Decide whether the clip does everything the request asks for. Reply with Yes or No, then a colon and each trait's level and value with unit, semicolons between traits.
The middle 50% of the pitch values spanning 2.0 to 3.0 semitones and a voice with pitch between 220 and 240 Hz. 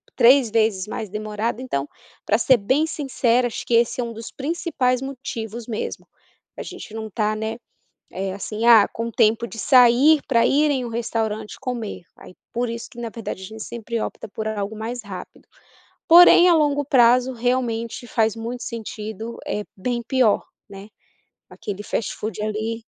Yes: narrow, 2.5 semitones; high, 230 Hz